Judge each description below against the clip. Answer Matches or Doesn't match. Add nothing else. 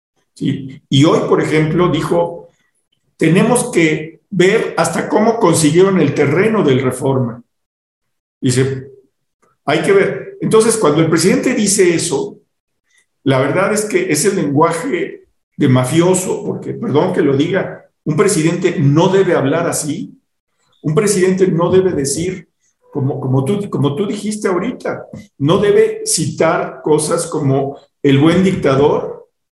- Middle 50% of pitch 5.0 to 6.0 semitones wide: Matches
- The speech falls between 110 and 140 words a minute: Matches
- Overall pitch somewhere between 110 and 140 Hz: Doesn't match